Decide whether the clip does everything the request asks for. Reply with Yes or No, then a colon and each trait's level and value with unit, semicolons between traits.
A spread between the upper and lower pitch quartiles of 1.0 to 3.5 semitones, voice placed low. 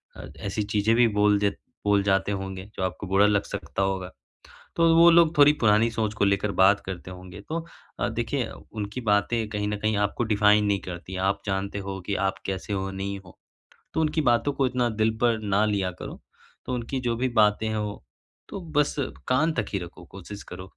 Yes: average, 3.1 semitones; low, 105 Hz